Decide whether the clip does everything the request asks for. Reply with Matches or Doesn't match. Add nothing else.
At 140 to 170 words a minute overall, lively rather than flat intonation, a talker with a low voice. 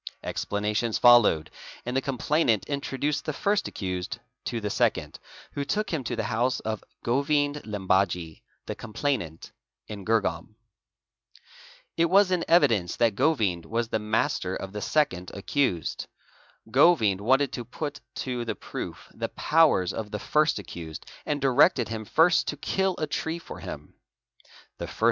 Matches